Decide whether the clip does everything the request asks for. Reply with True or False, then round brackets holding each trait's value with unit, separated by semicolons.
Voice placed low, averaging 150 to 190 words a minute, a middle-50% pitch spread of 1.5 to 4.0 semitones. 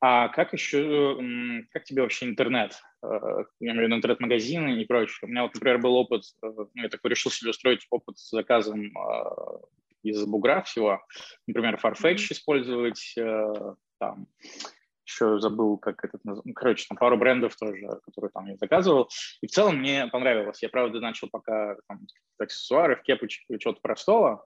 True (120 Hz; 160 wpm; 2.8 semitones)